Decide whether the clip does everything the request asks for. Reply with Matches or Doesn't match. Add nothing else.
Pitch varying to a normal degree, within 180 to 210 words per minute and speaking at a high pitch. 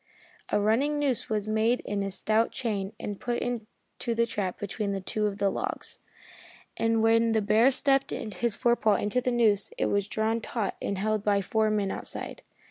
Doesn't match